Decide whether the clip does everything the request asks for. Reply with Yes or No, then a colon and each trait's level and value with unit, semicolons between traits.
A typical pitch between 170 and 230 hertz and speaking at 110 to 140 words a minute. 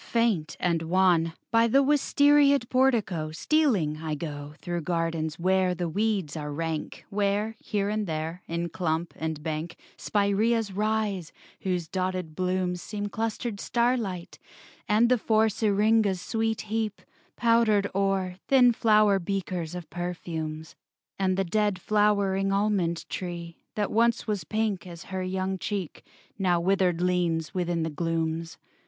Yes: high, 190 Hz; slow, 135 wpm